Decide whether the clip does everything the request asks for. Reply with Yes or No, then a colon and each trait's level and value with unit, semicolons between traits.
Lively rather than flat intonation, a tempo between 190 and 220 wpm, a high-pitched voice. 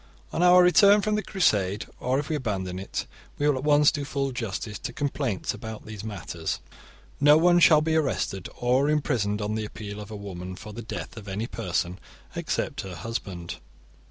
No: wide, 6.5 semitones; average, 195 wpm; low, 115 Hz